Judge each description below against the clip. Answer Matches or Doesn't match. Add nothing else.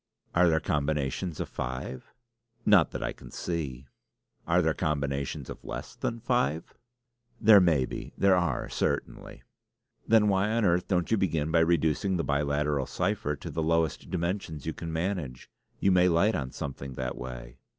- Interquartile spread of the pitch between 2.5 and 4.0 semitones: Doesn't match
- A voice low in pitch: Matches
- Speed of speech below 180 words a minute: Matches